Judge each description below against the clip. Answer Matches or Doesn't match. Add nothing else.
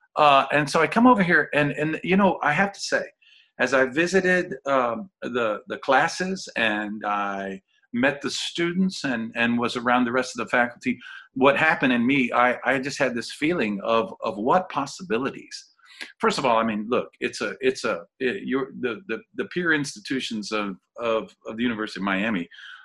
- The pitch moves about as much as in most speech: Doesn't match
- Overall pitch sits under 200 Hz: Matches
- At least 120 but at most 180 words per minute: Doesn't match